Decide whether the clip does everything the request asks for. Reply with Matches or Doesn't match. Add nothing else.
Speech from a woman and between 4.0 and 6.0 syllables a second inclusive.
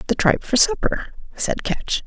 Matches